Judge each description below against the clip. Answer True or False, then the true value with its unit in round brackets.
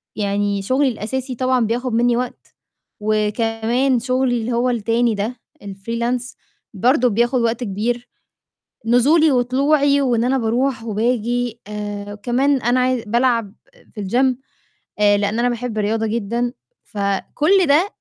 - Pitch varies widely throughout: False (2.8 semitones)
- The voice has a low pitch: False (240 Hz)